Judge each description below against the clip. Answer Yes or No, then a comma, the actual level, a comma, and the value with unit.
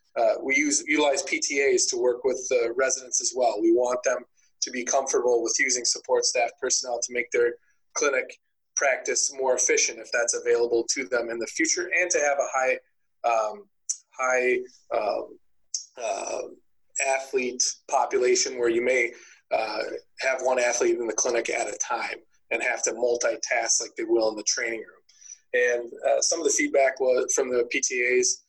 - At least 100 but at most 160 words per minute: No, average, 175 wpm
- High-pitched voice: Yes, very high, 380 Hz